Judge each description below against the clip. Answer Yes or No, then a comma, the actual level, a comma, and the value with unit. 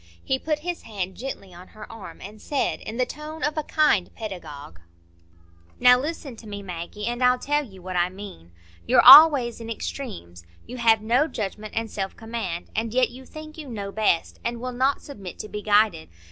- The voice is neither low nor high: No, high, 225 Hz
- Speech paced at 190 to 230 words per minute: Yes, average, 195 wpm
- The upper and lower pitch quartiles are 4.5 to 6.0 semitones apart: Yes, average, 5.0 semitones